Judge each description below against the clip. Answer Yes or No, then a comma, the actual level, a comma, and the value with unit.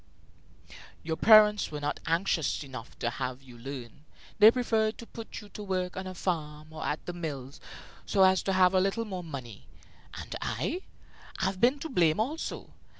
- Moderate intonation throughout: No, wide, 6.0 semitones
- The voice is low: No, medium, 180 Hz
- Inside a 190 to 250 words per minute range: No, average, 180 wpm